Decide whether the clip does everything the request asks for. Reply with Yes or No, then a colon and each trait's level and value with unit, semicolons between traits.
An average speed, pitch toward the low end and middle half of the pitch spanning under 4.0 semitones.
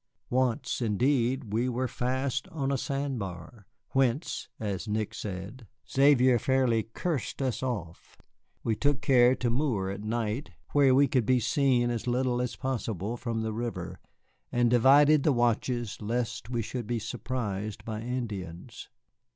Yes: average, 150 wpm; low, 120 Hz; average, 3.0 semitones